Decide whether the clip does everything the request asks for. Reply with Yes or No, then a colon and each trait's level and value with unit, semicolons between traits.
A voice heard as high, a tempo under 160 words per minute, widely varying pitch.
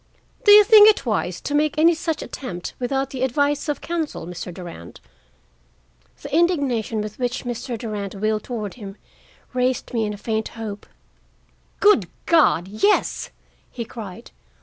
Yes: high, 245 Hz; average, 150 wpm; wide, 5.8 semitones